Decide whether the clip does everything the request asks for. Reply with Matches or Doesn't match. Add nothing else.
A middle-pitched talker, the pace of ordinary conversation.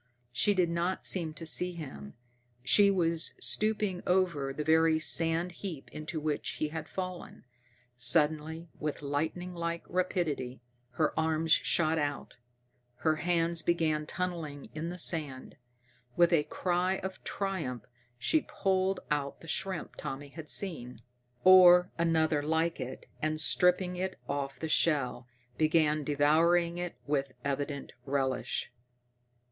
Doesn't match